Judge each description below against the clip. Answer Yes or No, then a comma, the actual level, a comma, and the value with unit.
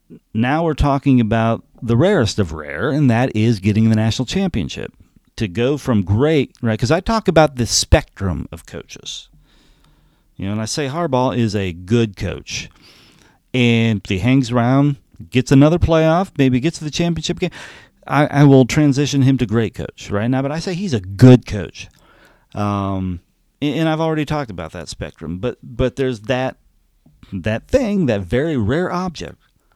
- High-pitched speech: No, low, 125 Hz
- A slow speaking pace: No, average, 175 wpm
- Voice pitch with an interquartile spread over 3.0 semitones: Yes, wide, 5.6 semitones